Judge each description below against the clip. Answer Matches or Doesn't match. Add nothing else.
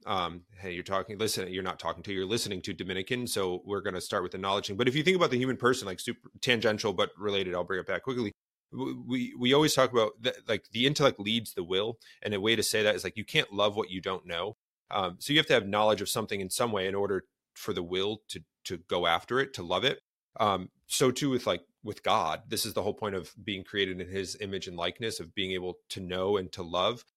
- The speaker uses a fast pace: Matches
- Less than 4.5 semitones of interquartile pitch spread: Doesn't match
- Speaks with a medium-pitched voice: Doesn't match